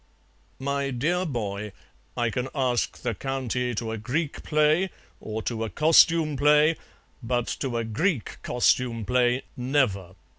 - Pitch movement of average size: Yes, average, 4.3 semitones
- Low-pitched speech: Yes, low, 125 Hz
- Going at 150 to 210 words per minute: No, average, 140 wpm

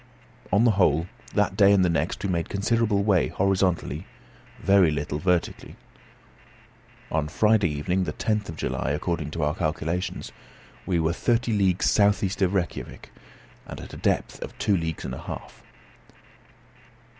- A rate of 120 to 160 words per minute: Yes, average, 155 wpm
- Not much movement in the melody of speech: No, average, 3.7 semitones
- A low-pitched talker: Yes, very low, 95 Hz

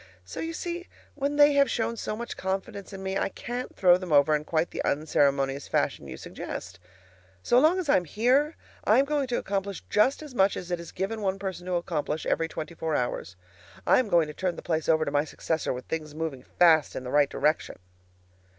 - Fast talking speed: Yes, fast, 225 wpm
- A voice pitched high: No, medium, 180 Hz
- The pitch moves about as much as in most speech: No, wide, 7.3 semitones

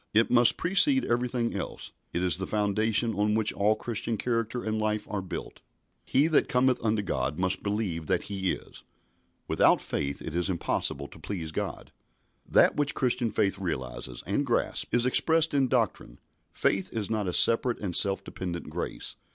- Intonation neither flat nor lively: Yes, average, 4.3 semitones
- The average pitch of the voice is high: No, low, 105 Hz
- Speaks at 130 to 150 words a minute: No, average, 175 wpm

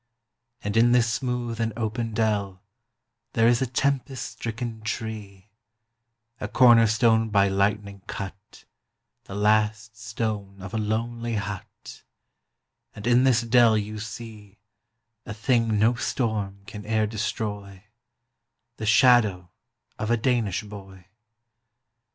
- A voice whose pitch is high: No, low, 110 Hz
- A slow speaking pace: Yes, slow, 125 wpm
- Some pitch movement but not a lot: No, narrow, 2.3 semitones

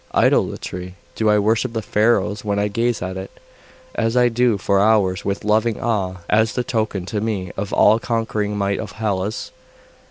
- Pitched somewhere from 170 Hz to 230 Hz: No, low, 105 Hz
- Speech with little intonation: Yes, narrow, 2.3 semitones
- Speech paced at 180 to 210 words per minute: Yes, average, 185 wpm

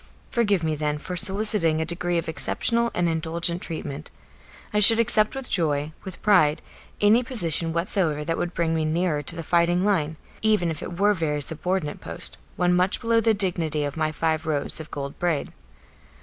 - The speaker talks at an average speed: Yes, average, 190 wpm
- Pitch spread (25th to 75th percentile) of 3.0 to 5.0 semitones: Yes, average, 3.9 semitones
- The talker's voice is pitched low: No, medium, 170 Hz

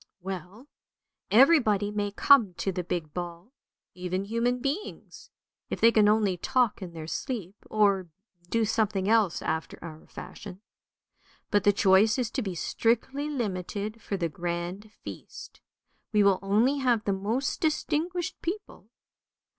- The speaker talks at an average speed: Yes, average, 145 wpm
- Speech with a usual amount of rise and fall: Yes, average, 4.2 semitones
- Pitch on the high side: Yes, high, 205 Hz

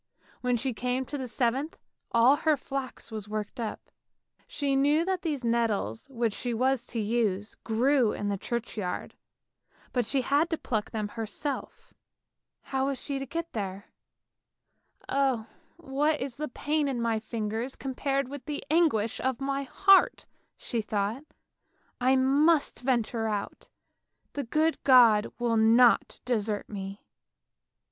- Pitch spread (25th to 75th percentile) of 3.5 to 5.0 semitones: Yes, average, 3.9 semitones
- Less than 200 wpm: Yes, average, 150 wpm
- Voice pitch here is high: Yes, very high, 250 Hz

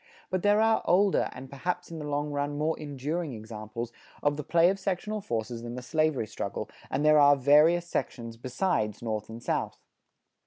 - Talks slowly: No, average, 185 wpm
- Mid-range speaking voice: Yes, medium, 145 Hz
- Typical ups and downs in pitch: No, wide, 6.3 semitones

